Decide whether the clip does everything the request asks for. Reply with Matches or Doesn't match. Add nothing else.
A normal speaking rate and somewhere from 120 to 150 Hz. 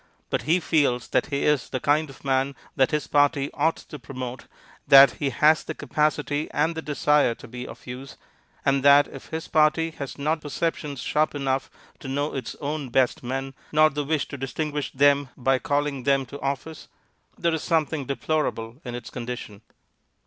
Matches